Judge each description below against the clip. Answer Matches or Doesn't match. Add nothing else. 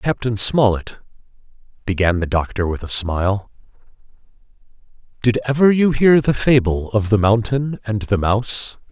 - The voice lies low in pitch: Matches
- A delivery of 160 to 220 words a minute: Doesn't match